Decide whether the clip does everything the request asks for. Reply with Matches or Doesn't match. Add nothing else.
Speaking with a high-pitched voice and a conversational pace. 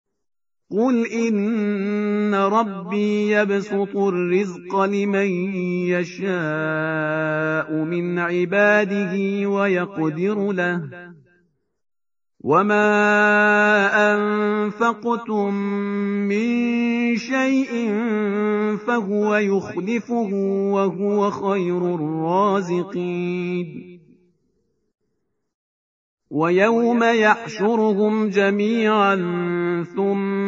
Doesn't match